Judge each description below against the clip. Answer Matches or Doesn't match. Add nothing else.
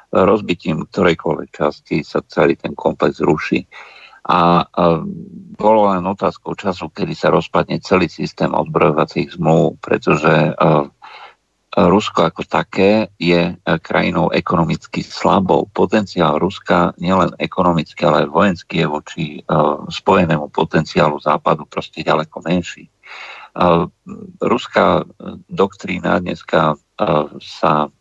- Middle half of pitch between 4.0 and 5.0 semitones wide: Doesn't match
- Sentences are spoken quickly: Doesn't match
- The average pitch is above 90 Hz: Doesn't match